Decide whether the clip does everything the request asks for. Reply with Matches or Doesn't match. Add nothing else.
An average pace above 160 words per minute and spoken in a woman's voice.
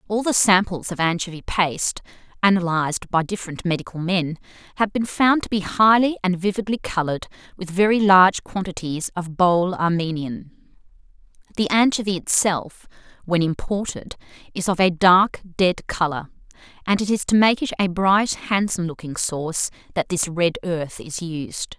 Doesn't match